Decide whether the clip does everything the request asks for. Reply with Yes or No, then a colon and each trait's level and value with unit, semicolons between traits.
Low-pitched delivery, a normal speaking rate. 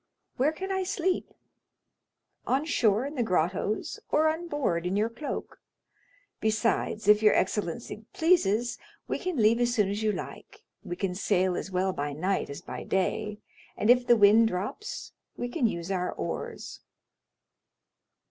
No: high, 215 Hz; average, 155 wpm